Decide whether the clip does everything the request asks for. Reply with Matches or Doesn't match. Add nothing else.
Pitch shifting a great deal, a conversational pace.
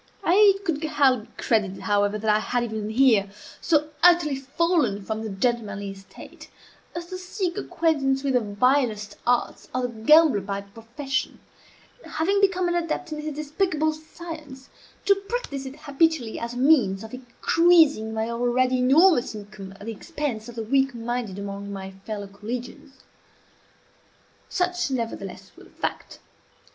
Matches